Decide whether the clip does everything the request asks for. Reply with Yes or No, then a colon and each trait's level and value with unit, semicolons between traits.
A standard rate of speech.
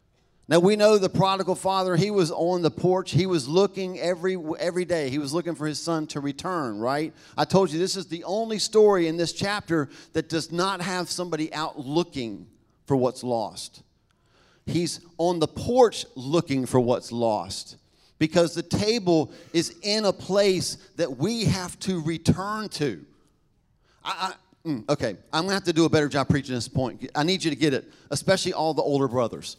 Yes: average, 190 wpm